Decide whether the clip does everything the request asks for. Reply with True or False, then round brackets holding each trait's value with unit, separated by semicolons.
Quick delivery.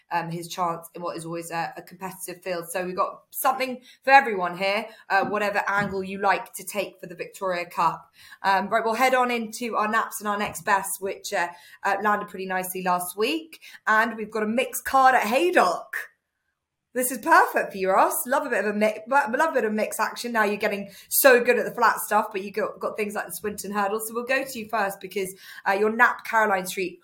True (235 wpm)